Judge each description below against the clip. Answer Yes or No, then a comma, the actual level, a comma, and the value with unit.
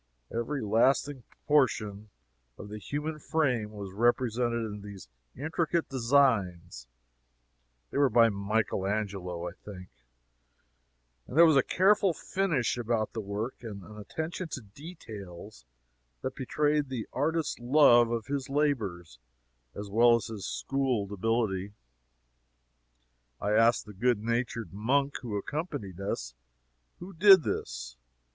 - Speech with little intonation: No, wide, 5.6 semitones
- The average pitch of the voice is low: Yes, low, 115 Hz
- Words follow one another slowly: Yes, slow, 125 wpm